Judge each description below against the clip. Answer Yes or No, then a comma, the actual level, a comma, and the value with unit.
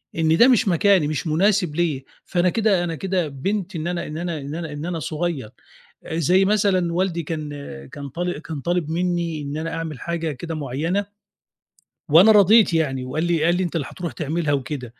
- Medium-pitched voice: Yes, medium, 165 Hz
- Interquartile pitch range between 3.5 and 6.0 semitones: No, average, 2.8 semitones